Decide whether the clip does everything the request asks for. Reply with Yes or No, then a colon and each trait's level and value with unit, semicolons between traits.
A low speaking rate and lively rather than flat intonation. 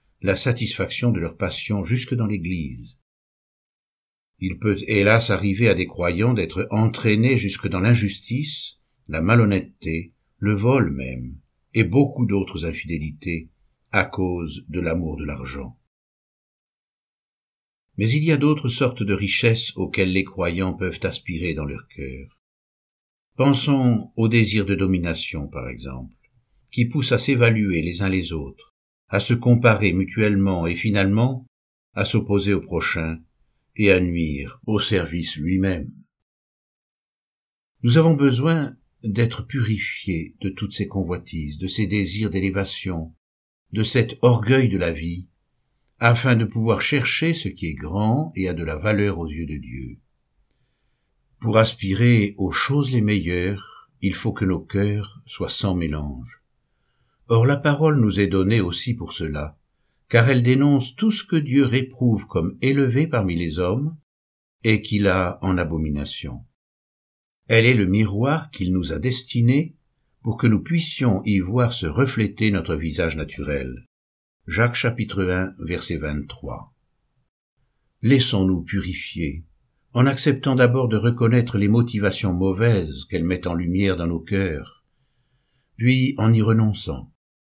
Yes: slow, 140 wpm; wide, 6.2 semitones